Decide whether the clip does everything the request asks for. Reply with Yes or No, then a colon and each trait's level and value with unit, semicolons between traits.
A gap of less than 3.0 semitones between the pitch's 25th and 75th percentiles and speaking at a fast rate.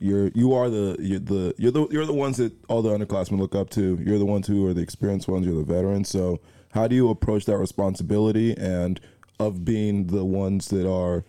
Yes: narrow, 2.5 semitones; fast, 230 wpm